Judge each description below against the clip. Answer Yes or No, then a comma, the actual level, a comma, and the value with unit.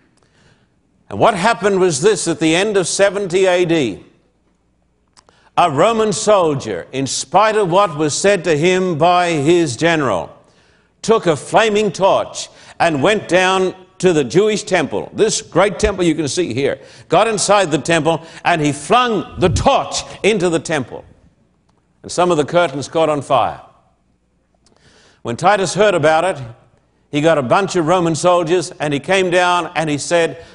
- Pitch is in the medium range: Yes, medium, 175 Hz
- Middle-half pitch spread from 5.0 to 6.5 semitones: No, average, 4.5 semitones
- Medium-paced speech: Yes, average, 160 wpm